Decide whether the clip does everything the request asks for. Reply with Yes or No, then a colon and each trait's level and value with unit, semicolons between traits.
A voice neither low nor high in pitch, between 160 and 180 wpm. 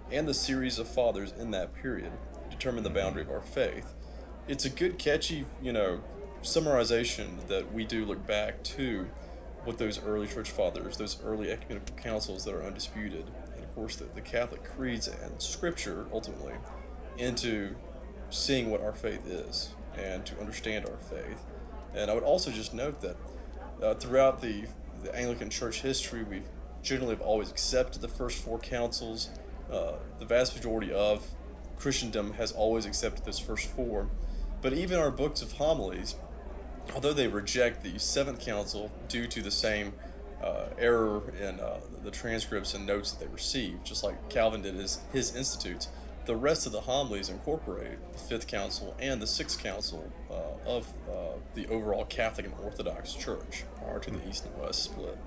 No: low, 105 Hz; average, 170 wpm